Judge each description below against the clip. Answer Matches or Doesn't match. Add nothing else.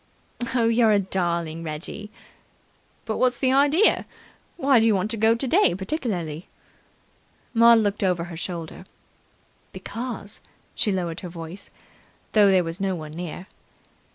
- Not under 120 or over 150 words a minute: Matches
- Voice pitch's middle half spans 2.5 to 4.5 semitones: Doesn't match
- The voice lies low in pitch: Doesn't match